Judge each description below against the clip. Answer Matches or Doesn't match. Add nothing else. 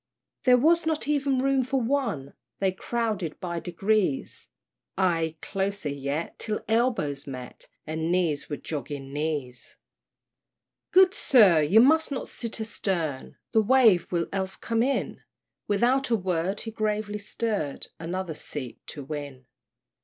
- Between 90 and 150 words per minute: Matches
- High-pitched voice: Matches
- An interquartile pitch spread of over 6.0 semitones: Matches